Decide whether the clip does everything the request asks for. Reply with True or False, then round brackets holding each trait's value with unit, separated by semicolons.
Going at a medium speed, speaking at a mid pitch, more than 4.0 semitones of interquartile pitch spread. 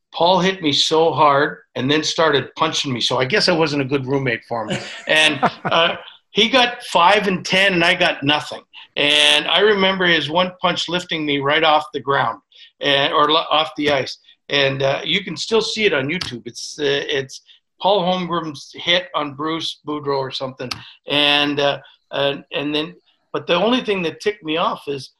True (195 wpm; 155 Hz; 4.4 semitones)